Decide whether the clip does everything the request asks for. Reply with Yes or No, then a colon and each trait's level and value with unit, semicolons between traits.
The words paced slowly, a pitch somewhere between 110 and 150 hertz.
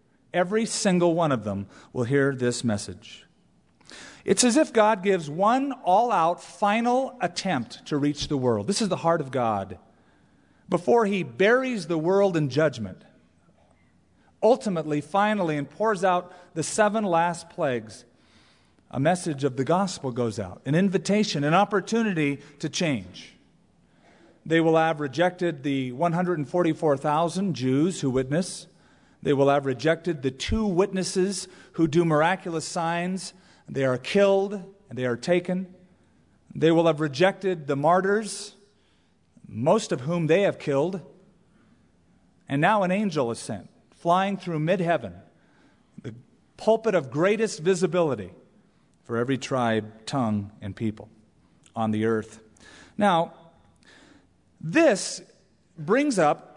No: slow, 130 wpm; medium, 165 Hz